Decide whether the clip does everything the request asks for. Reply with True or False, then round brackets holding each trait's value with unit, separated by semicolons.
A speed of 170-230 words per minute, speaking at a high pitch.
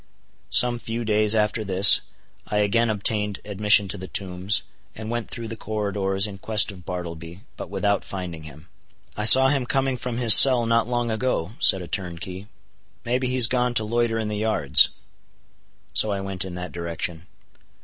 False (180 wpm; 105 Hz)